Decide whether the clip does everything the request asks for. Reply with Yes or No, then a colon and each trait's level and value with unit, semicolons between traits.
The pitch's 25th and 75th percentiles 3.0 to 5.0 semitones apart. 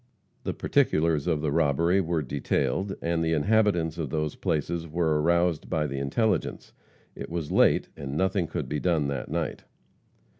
No: narrow, 2.5 semitones